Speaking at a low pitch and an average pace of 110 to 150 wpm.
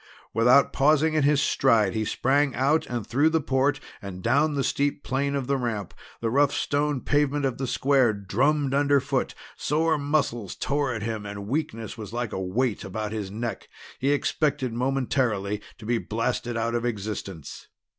No: low, 130 Hz; average, 175 wpm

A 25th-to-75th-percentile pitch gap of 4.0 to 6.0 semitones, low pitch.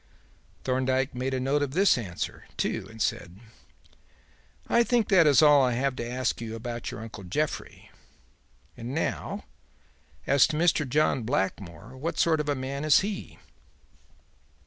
Yes: average, 4.3 semitones; low, 130 Hz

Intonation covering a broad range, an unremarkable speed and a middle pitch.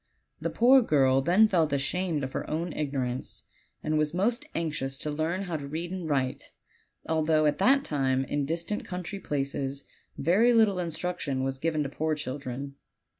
No: average, 4.5 semitones; average, 170 wpm; medium, 155 Hz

